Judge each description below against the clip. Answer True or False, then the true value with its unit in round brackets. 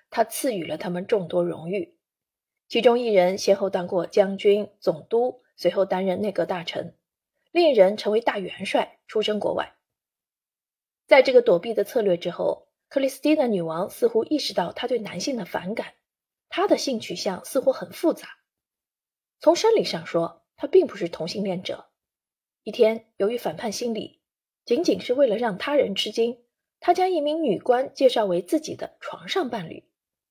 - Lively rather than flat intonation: True (6.9 semitones)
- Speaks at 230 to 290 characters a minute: True (255 characters per minute)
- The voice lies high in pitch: True (225 Hz)